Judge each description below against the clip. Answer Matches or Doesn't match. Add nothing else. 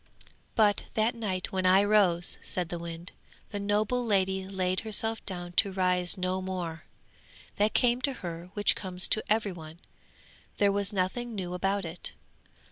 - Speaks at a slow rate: Doesn't match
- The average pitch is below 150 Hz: Doesn't match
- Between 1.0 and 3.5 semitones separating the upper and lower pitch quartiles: Matches